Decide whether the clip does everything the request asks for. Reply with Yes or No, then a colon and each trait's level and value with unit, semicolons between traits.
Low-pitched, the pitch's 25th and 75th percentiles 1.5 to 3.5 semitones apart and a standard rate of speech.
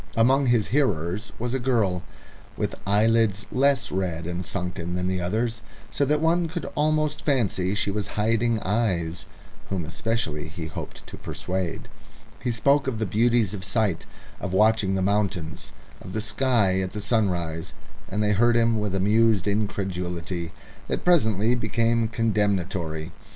No: low, 105 Hz; average, 4.2 semitones; average, 150 wpm